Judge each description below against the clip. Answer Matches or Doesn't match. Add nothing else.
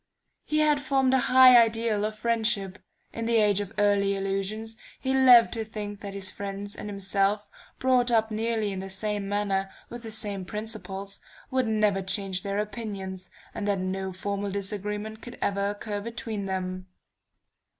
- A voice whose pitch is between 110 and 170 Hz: Doesn't match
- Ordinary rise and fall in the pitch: Doesn't match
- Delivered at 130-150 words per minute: Doesn't match